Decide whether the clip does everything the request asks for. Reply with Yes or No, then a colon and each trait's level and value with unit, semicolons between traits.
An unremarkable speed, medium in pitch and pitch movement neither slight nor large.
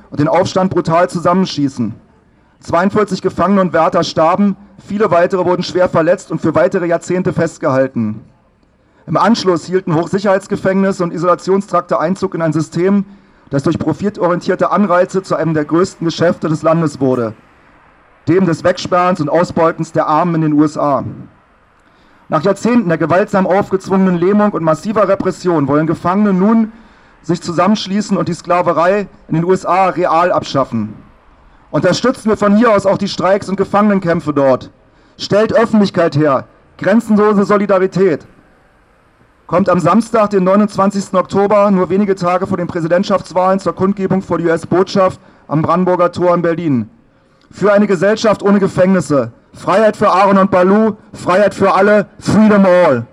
Yes: average, 145 wpm; medium, 180 Hz; average, 3.0 semitones